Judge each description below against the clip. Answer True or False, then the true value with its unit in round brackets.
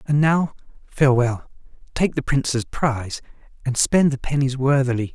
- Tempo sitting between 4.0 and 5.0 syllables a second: True (4.9 syllables/s)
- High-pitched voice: False (135 Hz)